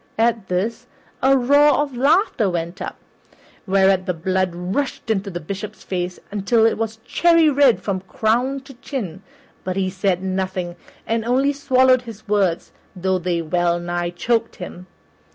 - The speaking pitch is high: Yes, high, 200 Hz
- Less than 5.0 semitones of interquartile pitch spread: No, wide, 5.4 semitones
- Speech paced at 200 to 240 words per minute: No, average, 155 wpm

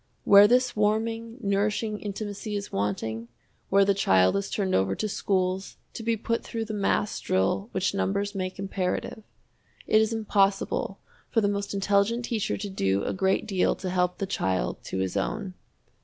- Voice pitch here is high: Yes, high, 200 Hz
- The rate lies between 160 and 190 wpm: Yes, average, 170 wpm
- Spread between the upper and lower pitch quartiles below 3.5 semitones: Yes, narrow, 2.5 semitones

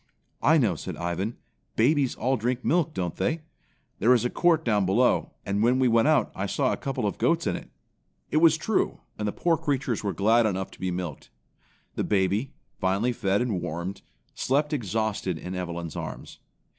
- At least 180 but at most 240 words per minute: Yes, average, 190 wpm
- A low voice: Yes, low, 110 Hz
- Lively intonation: Yes, wide, 5.8 semitones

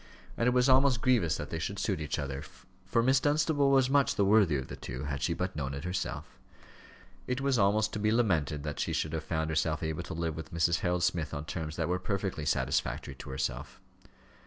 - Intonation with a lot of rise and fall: Yes, wide, 6.7 semitones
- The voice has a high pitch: No, very low, 90 Hz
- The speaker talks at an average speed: No, fast, 225 wpm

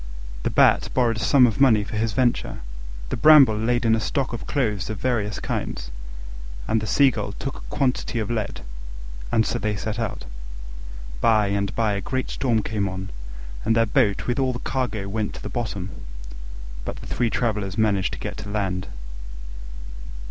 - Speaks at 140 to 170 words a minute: No, average, 180 wpm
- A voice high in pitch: No, low, 110 Hz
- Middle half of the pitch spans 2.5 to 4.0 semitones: Yes, average, 3.1 semitones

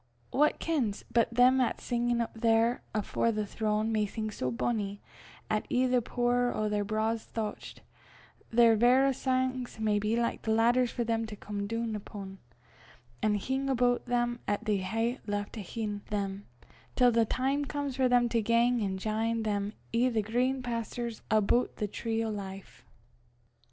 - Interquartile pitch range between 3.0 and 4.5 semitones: No, narrow, 2.6 semitones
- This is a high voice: Yes, high, 230 Hz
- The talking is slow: No, average, 165 wpm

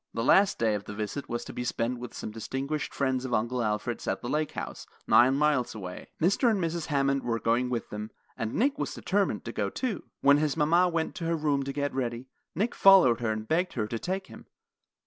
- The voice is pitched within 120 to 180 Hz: Yes, low, 135 Hz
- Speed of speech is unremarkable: No, fast, 230 wpm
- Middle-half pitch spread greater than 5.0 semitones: Yes, wide, 5.5 semitones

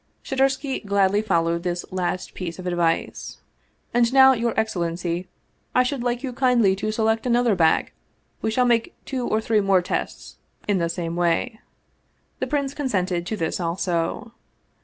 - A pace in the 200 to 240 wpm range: No, average, 160 wpm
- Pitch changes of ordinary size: No, wide, 5.7 semitones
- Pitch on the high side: Yes, high, 210 Hz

